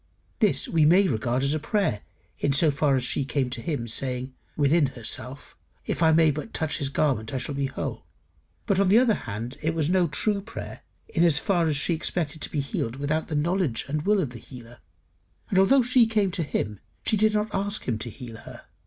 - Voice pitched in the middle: Yes, medium, 150 Hz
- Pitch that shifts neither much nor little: No, wide, 6.1 semitones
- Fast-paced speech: Yes, fast, 220 wpm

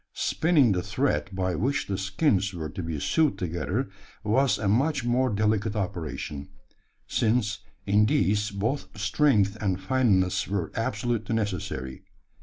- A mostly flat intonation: No, average, 4.3 semitones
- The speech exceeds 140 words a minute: No, slow, 135 wpm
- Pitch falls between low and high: No, low, 105 Hz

